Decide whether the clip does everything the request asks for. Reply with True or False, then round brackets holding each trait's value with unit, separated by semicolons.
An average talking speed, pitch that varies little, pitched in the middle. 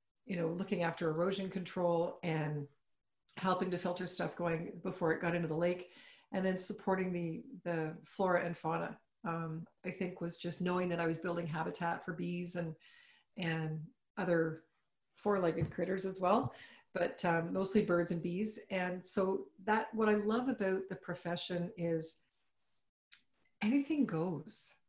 True (155 wpm; 2.2 semitones; 175 Hz)